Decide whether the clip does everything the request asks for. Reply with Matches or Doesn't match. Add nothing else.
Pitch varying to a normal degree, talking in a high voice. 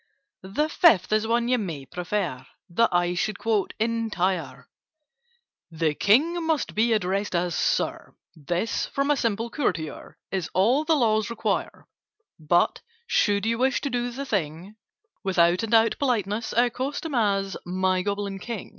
Matches